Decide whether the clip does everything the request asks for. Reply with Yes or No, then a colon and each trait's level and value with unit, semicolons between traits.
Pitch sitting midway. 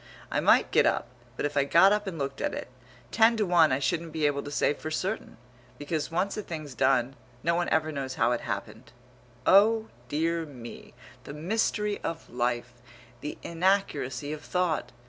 Yes: medium, 155 Hz